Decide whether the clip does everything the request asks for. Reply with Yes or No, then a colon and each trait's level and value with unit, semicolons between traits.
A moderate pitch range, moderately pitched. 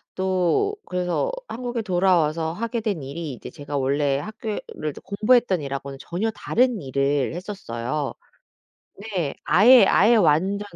No: wide, 6.8 semitones; medium, 180 Hz